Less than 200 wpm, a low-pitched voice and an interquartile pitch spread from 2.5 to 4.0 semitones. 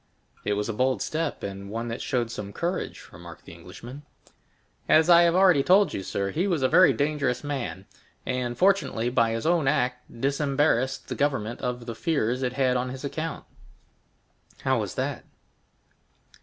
No: average, 170 wpm; low, 130 Hz; average, 4.7 semitones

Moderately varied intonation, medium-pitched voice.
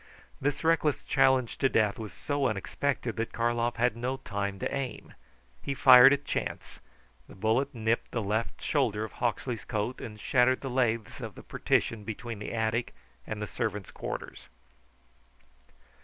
No: average, 3.1 semitones; low, 115 Hz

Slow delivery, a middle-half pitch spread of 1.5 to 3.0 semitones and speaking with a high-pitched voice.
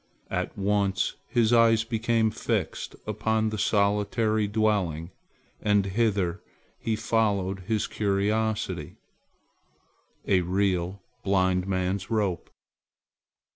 No: slow, 95 wpm; narrow, 2.5 semitones; low, 100 Hz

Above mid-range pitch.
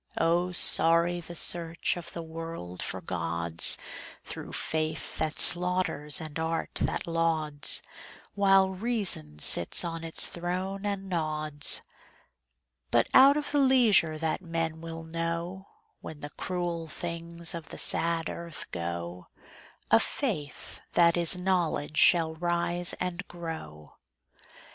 No: medium, 165 Hz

